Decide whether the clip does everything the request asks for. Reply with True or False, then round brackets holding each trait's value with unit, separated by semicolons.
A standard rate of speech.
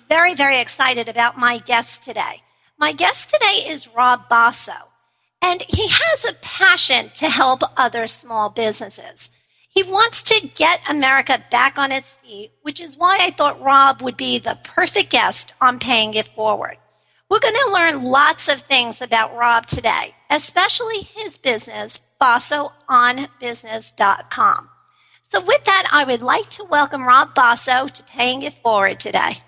True (155 wpm)